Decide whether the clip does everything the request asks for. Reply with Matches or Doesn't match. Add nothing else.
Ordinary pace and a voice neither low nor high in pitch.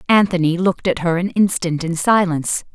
Matches